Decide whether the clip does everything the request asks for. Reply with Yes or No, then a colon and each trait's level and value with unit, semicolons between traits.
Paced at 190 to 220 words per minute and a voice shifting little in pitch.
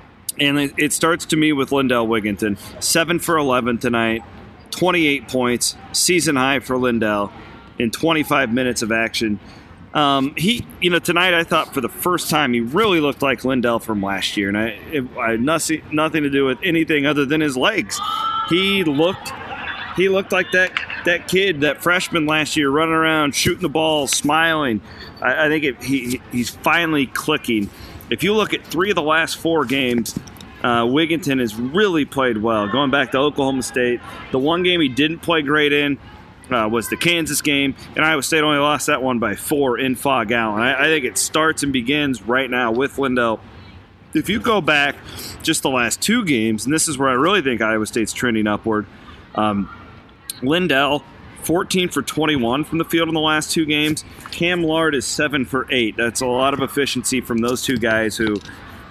No: average, 195 wpm; average, 5.3 semitones